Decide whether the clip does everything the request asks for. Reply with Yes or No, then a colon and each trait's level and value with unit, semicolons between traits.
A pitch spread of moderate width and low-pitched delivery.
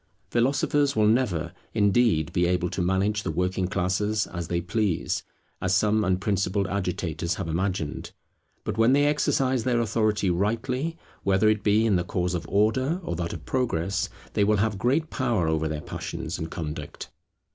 Yes: average, 4.2 semitones; low, 100 Hz